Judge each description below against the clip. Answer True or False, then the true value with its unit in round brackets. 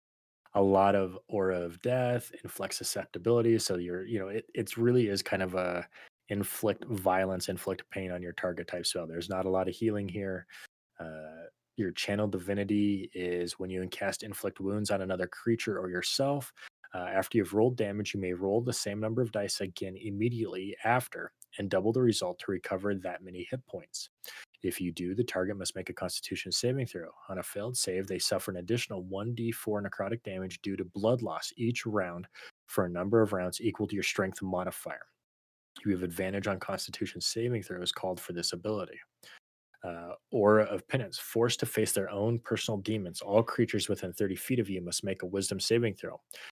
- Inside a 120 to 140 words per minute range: False (190 wpm)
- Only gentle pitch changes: False (3.3 semitones)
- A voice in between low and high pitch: False (100 Hz)